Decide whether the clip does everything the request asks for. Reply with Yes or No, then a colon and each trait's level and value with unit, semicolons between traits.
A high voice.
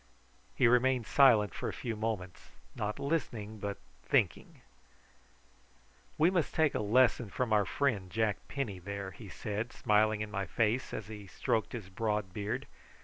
No: low, 110 Hz